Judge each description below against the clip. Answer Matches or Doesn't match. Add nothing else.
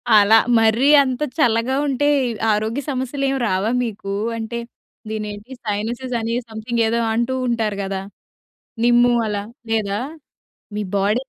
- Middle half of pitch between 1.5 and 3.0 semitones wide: Matches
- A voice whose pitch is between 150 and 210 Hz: Doesn't match